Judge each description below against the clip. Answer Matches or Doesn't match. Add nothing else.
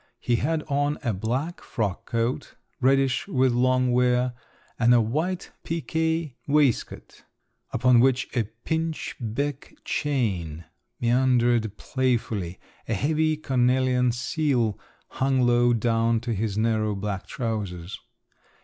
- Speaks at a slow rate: Matches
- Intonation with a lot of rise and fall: Doesn't match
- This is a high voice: Doesn't match